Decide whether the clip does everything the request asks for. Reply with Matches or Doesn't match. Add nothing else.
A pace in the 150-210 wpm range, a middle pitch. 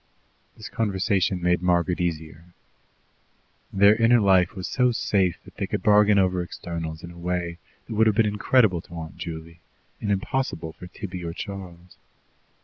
Doesn't match